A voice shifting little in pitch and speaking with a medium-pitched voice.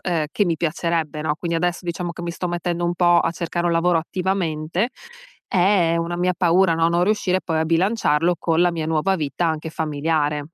Yes: narrow, 1.7 semitones; medium, 170 Hz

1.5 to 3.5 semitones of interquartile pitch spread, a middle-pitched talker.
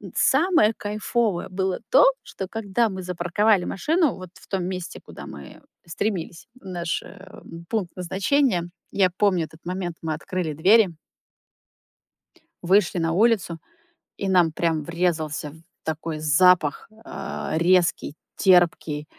Yes: average, 3.2 semitones; medium, 180 Hz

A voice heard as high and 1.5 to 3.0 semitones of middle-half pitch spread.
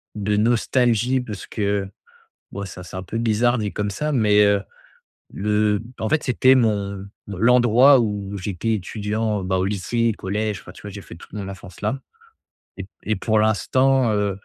No: low, 105 Hz; narrow, 2.6 semitones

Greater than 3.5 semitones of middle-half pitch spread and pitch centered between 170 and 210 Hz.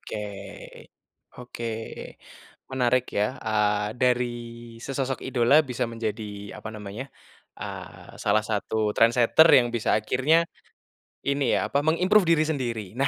No: average, 3.9 semitones; low, 120 Hz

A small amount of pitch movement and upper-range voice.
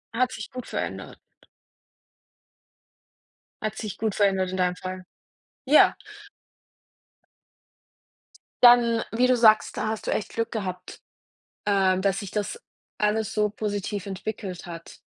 No: average, 3.0 semitones; high, 210 Hz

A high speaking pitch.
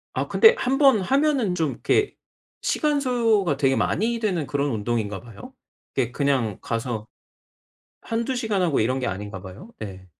No: medium, 145 Hz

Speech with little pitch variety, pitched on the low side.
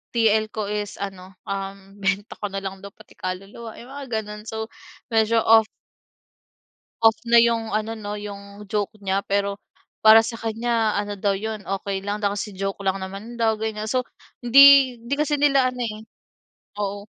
No: narrow, 2.2 semitones; high, 210 Hz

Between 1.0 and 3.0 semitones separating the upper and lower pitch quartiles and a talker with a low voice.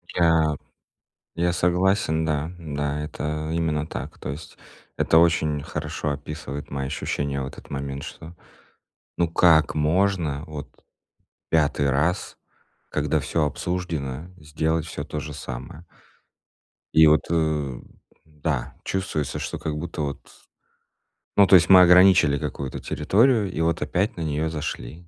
Yes: average, 2.7 semitones; very low, 80 Hz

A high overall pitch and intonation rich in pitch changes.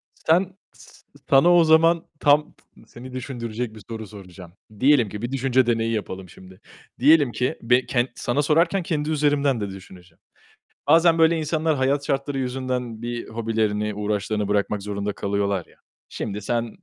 No: low, 120 Hz; wide, 5.8 semitones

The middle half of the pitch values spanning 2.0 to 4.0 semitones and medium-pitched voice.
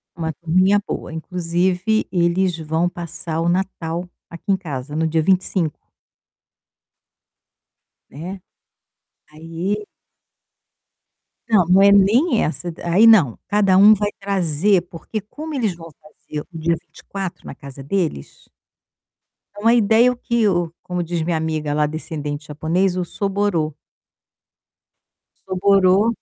Yes: average, 3.6 semitones; medium, 180 Hz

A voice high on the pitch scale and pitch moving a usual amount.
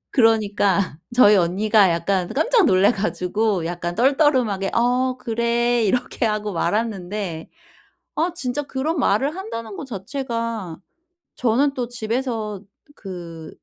Yes: high, 220 Hz; average, 4.7 semitones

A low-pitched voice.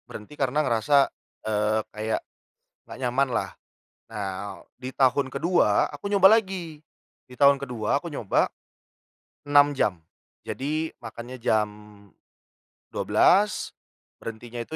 Yes: low, 130 Hz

